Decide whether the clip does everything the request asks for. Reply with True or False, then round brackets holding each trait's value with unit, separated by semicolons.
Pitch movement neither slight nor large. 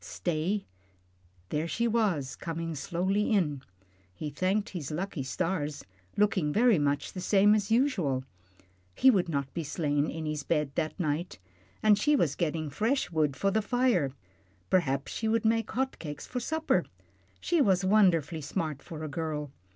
False (5.9 semitones)